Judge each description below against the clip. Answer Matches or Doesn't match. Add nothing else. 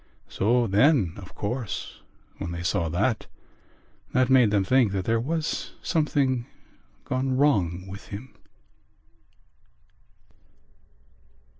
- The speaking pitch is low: Matches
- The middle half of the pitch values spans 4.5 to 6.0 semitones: Matches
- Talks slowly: Matches